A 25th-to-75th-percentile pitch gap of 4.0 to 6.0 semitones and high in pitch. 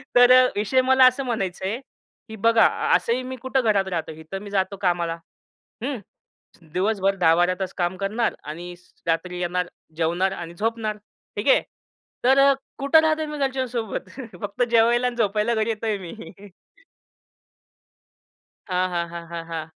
Yes: average, 5.3 semitones; high, 205 Hz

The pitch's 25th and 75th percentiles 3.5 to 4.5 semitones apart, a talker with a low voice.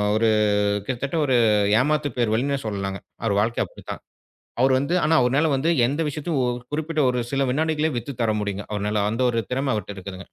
No: average, 5.0 semitones; low, 125 Hz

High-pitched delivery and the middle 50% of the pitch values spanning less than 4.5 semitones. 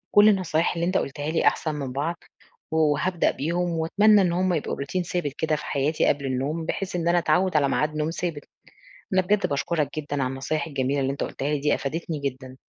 No: medium, 155 Hz; average, 3.5 semitones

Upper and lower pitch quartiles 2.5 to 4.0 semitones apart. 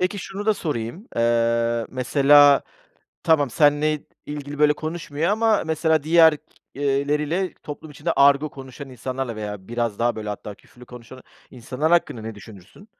No: average, 5.0 semitones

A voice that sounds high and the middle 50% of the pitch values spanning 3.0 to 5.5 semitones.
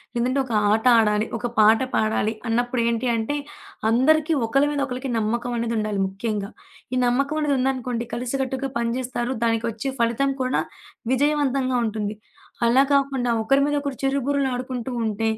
Yes: high, 245 Hz; average, 3.3 semitones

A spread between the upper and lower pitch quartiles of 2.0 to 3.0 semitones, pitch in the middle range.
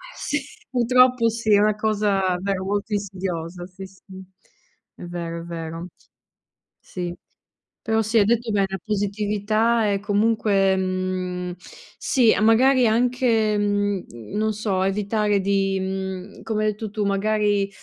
No: narrow, 2.4 semitones; high, 205 Hz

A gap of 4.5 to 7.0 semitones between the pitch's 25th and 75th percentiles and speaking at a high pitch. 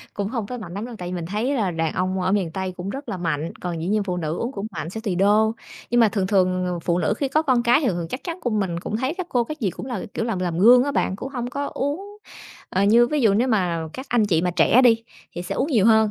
Yes: wide, 5.4 semitones; high, 210 Hz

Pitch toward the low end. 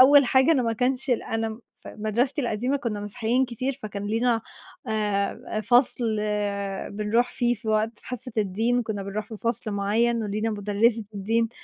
No: high, 225 Hz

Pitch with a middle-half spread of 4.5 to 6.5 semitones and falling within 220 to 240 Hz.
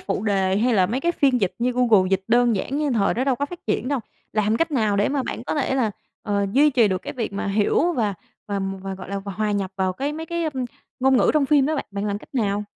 Yes: average, 5.2 semitones; high, 225 Hz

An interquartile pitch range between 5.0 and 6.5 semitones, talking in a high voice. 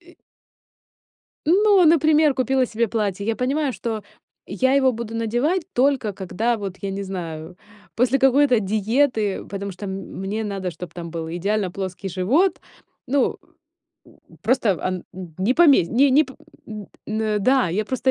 Yes: wide, 5.6 semitones; high, 220 Hz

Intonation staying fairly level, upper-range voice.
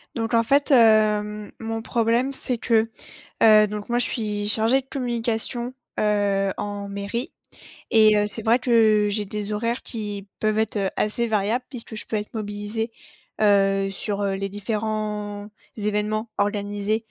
Yes: narrow, 1.8 semitones; high, 215 Hz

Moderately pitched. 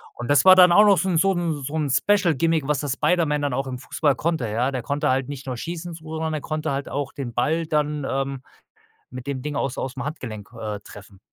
Yes: medium, 145 Hz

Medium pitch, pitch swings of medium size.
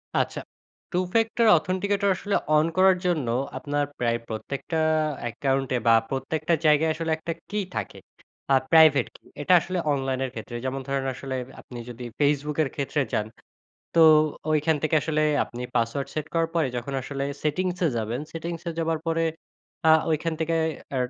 Yes: medium, 150 Hz; average, 3.8 semitones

